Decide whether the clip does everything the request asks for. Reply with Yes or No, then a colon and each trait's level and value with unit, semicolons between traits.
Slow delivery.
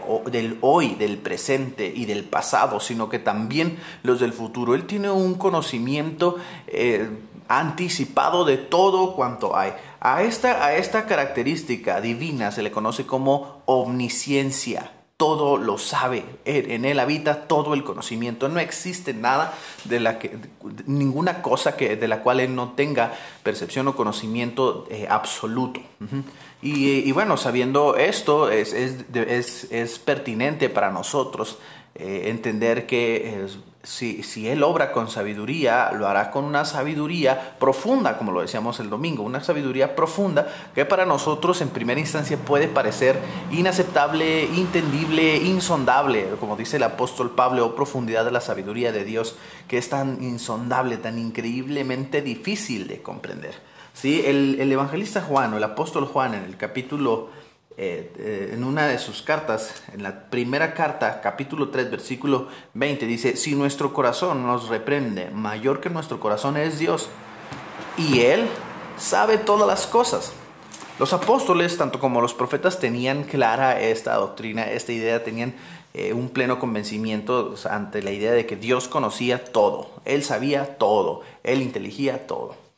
No: average, 155 wpm